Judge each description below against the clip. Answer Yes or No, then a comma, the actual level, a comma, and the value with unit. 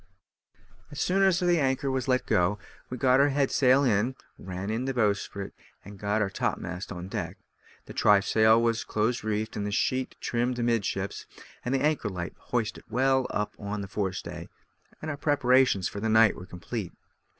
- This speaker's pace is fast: No, average, 180 wpm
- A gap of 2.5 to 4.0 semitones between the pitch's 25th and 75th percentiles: No, average, 4.5 semitones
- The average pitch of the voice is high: No, low, 115 Hz